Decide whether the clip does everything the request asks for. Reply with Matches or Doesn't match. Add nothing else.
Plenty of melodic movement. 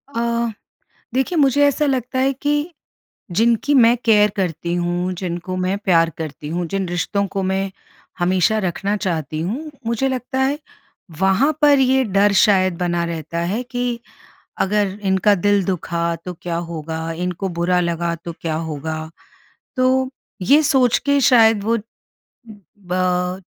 Matches